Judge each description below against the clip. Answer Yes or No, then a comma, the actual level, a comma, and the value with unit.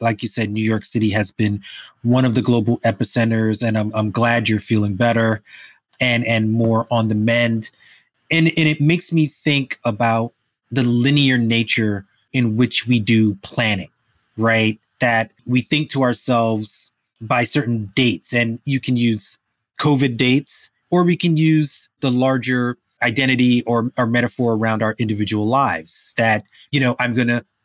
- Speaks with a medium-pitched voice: No, low, 120 Hz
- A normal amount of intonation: No, narrow, 2.3 semitones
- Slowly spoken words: No, average, 165 wpm